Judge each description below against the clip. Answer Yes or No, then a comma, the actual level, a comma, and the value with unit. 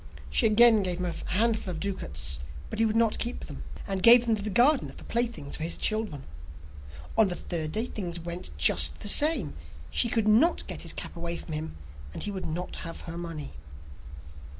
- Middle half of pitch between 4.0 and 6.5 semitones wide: Yes, average, 5.2 semitones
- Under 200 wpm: No, fast, 205 wpm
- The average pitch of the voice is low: No, high, 195 Hz